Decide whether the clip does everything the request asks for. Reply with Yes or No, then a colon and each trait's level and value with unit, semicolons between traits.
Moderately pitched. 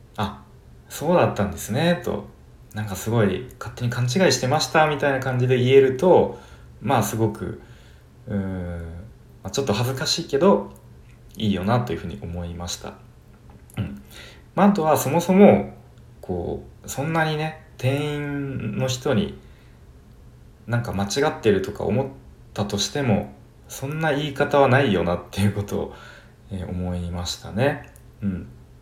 No: low, 120 Hz